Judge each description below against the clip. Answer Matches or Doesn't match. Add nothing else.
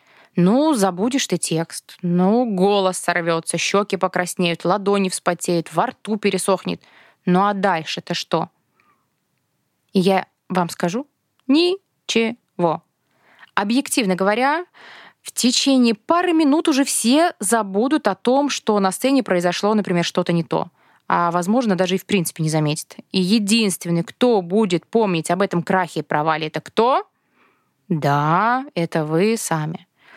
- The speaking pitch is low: Doesn't match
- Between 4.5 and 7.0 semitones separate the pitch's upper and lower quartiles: Matches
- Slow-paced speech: Doesn't match